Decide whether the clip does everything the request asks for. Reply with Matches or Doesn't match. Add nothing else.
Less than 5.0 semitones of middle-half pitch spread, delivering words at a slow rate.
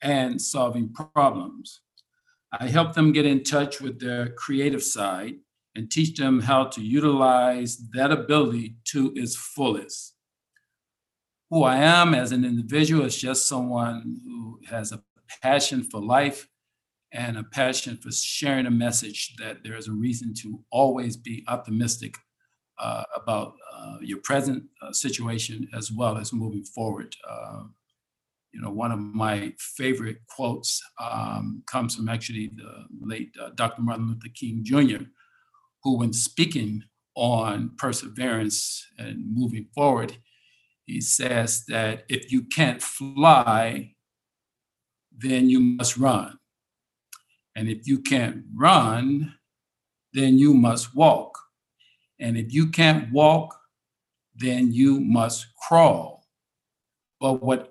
Matches